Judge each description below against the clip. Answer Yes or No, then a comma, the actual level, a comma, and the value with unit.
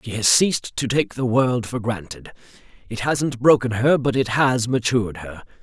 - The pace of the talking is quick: No, average, 190 wpm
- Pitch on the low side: Yes, low, 120 Hz